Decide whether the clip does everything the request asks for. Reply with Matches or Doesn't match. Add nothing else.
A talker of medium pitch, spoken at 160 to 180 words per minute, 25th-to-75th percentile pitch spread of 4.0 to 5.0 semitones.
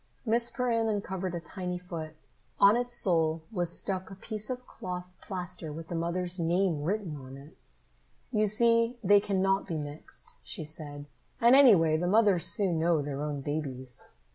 Matches